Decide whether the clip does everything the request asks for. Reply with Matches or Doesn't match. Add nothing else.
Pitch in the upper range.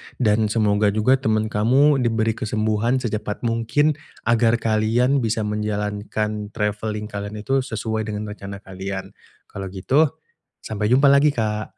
Doesn't match